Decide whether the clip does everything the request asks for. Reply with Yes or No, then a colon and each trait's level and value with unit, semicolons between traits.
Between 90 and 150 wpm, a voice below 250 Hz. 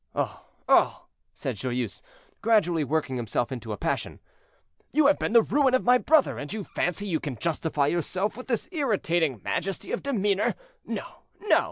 No: average, 170 wpm; medium, 185 Hz